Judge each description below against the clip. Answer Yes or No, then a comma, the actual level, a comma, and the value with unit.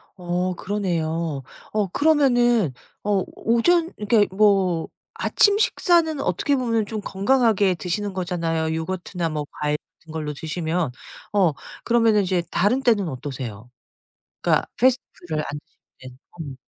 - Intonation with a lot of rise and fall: Yes, wide, 5.9 semitones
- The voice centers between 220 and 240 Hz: No, high, 190 Hz